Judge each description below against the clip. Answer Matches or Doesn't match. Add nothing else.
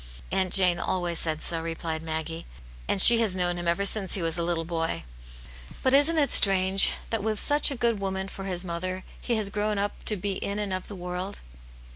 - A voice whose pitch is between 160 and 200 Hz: Matches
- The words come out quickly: Matches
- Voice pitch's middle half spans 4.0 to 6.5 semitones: Doesn't match